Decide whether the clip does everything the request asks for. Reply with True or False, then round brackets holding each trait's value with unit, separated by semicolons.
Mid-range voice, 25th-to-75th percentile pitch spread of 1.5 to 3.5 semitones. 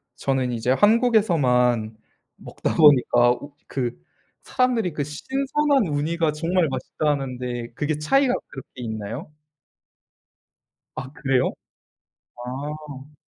False (145 Hz; 5.2 semitones)